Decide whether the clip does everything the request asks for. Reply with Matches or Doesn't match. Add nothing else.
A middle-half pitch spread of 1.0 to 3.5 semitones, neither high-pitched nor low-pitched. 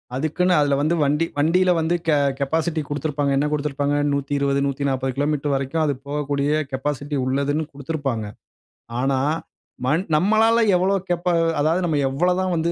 Matches